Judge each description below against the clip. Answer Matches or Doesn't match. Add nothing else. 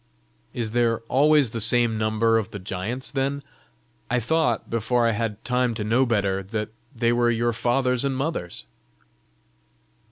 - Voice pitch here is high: Doesn't match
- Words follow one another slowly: Doesn't match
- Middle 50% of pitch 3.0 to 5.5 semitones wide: Doesn't match